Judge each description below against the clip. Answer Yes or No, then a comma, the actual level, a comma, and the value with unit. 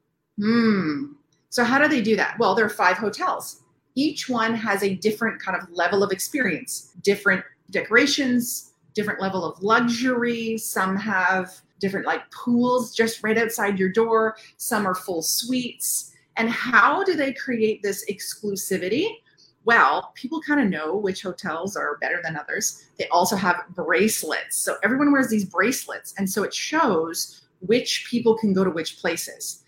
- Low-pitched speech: No, high, 210 Hz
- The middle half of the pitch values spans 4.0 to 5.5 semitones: Yes, average, 4.6 semitones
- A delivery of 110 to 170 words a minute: Yes, average, 160 wpm